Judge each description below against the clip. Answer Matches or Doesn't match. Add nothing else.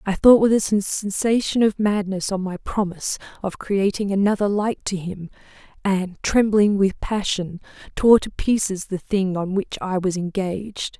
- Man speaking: Doesn't match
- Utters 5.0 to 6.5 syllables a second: Doesn't match